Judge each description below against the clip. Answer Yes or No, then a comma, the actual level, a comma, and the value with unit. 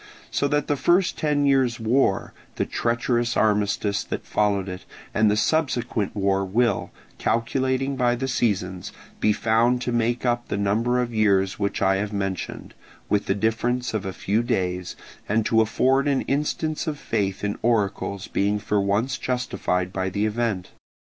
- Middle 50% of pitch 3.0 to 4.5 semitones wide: Yes, average, 3.8 semitones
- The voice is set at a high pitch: No, low, 110 Hz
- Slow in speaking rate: No, average, 165 wpm